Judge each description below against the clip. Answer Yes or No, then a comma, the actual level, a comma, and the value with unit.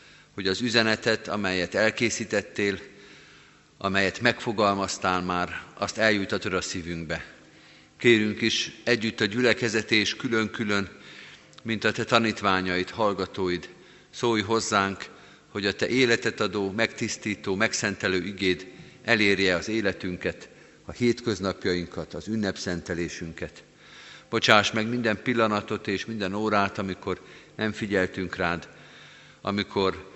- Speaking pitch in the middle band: No, low, 100 Hz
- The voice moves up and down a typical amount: Yes, average, 3.0 semitones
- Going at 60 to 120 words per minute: Yes, slow, 105 wpm